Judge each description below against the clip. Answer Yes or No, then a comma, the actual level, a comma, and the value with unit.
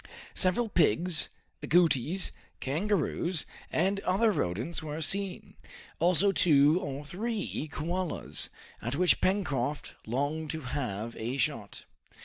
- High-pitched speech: No, medium, 160 Hz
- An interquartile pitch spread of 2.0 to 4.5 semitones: No, average, 4.9 semitones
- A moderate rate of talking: No, slow, 110 wpm